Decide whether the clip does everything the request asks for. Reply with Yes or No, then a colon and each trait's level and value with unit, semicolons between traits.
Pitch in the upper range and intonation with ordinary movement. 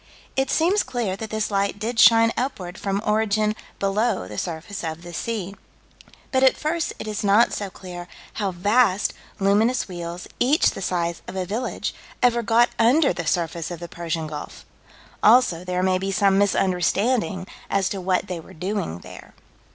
Yes: high, 200 Hz; average, 4.1 semitones